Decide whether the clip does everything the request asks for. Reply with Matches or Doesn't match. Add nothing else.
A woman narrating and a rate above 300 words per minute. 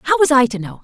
Matches